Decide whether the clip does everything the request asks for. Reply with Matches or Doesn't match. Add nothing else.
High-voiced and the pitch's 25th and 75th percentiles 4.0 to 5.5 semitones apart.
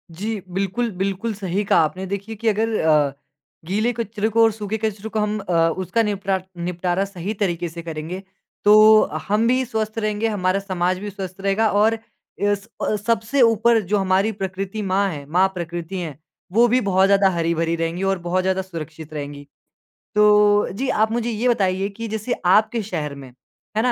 Doesn't match